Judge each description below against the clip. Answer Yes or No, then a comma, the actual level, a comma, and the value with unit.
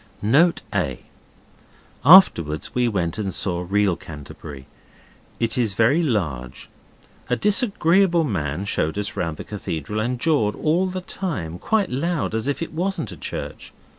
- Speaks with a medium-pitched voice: No, low, 110 Hz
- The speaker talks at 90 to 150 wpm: Yes, average, 145 wpm